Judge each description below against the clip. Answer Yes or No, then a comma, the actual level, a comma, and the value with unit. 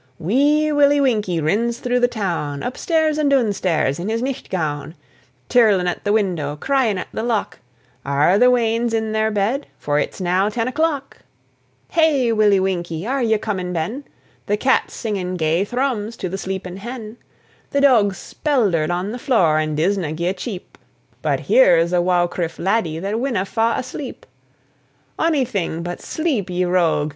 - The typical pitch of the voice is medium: No, high, 210 Hz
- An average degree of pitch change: No, wide, 5.9 semitones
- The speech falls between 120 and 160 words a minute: No, average, 170 wpm